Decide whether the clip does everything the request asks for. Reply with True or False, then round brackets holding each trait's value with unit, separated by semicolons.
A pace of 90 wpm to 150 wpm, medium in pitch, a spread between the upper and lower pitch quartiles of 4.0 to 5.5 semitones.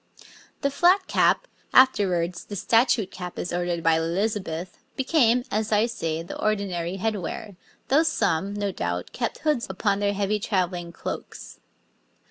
False (145 wpm; 200 Hz; 4.5 semitones)